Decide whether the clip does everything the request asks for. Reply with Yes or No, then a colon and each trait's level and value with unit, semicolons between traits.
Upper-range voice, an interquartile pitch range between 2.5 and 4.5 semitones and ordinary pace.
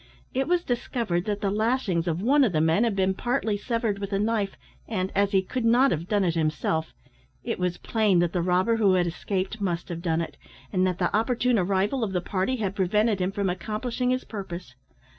No: high, 200 Hz; average, 4.1 semitones; fast, 215 wpm